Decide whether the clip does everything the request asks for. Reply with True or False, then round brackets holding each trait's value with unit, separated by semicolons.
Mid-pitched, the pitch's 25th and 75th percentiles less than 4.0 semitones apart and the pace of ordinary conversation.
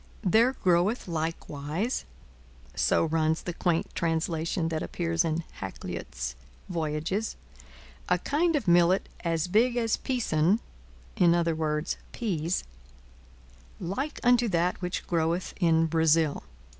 False (170 Hz; 3.4 semitones; 105 wpm)